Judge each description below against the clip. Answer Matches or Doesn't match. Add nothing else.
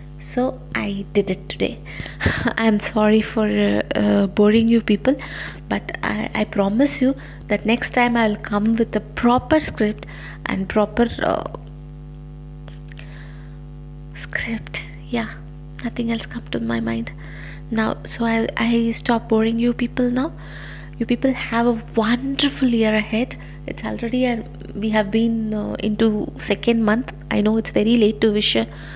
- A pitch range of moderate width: Doesn't match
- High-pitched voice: Matches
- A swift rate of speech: Matches